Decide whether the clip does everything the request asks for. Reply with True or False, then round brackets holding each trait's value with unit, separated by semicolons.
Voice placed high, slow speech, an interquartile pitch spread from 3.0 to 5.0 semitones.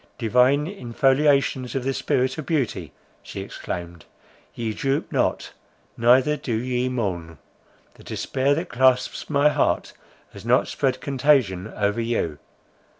False (125 Hz; 130 wpm; 3.6 semitones)